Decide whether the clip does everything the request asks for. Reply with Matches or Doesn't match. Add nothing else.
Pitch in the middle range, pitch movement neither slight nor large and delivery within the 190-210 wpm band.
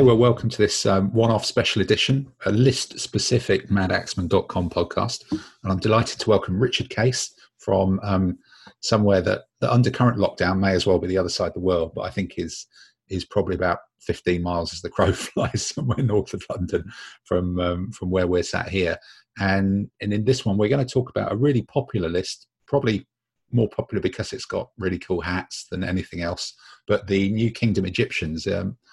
Doesn't match